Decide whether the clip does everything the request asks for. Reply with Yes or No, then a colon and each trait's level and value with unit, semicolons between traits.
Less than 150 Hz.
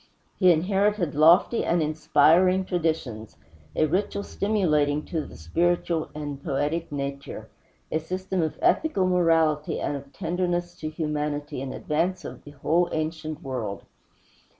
No: medium, 160 Hz